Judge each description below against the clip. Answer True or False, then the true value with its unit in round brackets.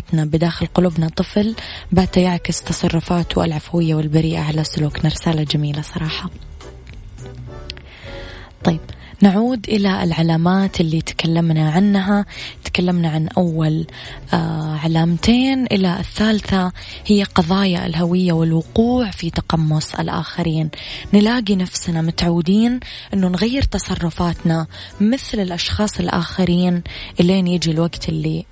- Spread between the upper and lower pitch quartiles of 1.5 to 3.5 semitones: True (2.9 semitones)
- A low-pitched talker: False (170 Hz)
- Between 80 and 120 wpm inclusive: True (95 wpm)